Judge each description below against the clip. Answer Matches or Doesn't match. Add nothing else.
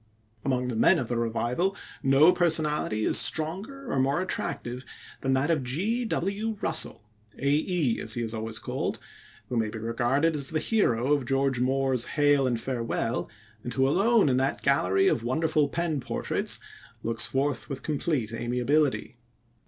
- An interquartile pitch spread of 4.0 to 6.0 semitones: Matches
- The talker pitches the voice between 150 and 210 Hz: Doesn't match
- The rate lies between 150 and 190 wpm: Matches